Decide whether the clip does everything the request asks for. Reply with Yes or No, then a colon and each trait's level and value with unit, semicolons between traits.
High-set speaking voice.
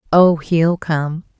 No: medium, 165 Hz